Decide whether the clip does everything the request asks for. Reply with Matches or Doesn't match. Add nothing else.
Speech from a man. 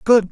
Matches